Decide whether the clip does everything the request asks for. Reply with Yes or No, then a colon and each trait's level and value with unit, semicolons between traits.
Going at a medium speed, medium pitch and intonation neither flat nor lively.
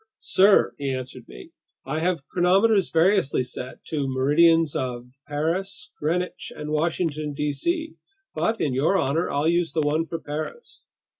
Yes: average, 150 wpm; medium, 155 Hz; average, 4.2 semitones